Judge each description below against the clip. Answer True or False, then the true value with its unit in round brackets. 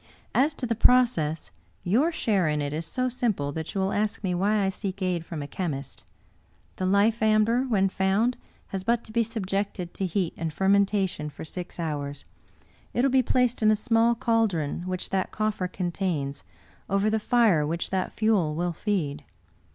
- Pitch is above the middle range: True (195 Hz)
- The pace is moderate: True (180 wpm)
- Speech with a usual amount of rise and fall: True (4.7 semitones)